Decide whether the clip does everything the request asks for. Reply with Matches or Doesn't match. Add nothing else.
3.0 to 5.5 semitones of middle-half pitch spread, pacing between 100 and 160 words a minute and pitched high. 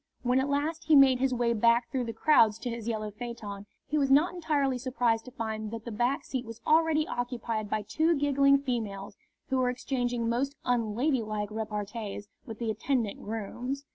Doesn't match